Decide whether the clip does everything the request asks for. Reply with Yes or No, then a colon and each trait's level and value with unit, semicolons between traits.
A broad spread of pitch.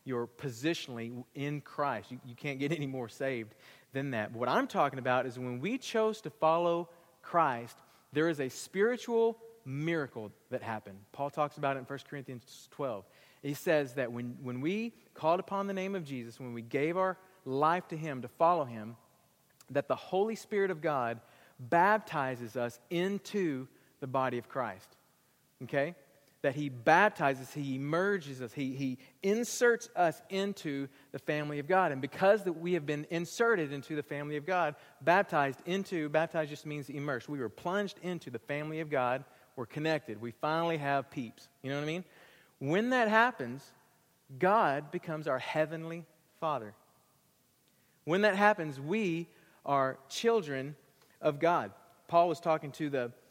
No: average, 4.6 semitones